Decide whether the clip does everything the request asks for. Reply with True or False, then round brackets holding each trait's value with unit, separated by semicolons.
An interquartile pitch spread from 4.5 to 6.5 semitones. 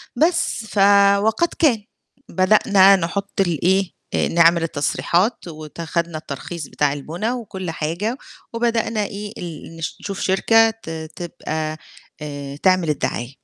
True (5.1 semitones)